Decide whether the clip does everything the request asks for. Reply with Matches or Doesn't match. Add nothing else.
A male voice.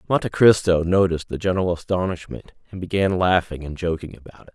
Matches